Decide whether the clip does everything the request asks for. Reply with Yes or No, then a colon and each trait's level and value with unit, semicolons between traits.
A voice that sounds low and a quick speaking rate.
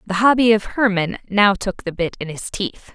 No: high, 200 Hz; fast, 225 wpm